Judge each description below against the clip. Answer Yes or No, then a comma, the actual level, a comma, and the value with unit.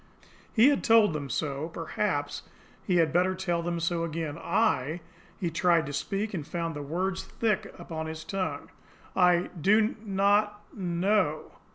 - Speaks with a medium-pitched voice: Yes, medium, 175 Hz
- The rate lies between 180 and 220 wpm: No, average, 160 wpm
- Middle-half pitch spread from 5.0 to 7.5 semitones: No, average, 3.8 semitones